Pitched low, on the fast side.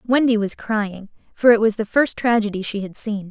No: high, 220 Hz; fast, 220 wpm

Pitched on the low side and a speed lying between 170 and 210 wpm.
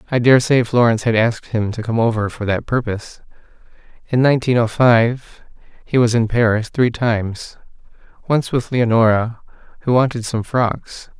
No: low, 115 Hz; average, 150 wpm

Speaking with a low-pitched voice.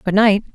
No: high, 205 Hz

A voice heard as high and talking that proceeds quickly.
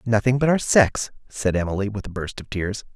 No: low, 110 Hz; fast, 225 wpm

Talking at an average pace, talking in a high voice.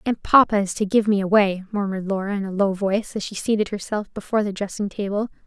No: fast, 230 wpm; high, 200 Hz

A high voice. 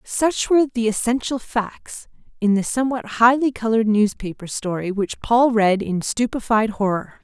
Yes: high, 225 Hz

